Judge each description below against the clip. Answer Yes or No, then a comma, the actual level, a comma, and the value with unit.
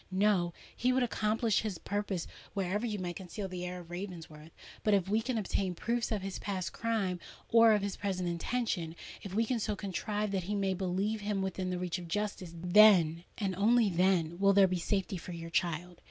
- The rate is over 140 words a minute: Yes, average, 190 wpm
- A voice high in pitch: Yes, high, 195 Hz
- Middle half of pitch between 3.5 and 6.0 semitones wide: No, average, 2.9 semitones